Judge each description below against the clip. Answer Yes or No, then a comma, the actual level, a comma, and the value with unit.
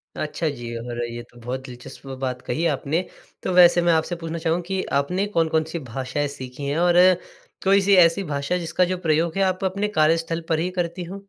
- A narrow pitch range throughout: No, average, 4.1 semitones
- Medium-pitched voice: Yes, medium, 165 Hz